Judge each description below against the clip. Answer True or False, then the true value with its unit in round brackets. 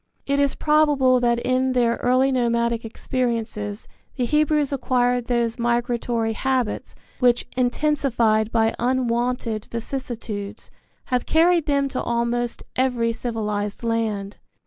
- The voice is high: True (240 Hz)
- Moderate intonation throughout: False (2.1 semitones)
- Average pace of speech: False (115 wpm)